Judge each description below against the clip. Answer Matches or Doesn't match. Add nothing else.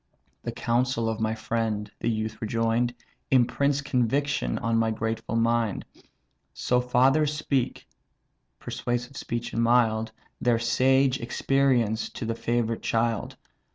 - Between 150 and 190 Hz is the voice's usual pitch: Doesn't match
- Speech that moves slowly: Matches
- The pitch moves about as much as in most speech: Doesn't match